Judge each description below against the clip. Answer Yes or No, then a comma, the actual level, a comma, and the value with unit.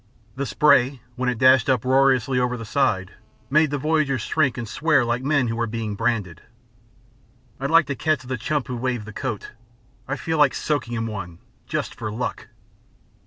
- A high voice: No, low, 130 Hz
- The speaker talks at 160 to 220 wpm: Yes, average, 180 wpm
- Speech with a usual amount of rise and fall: Yes, average, 3.6 semitones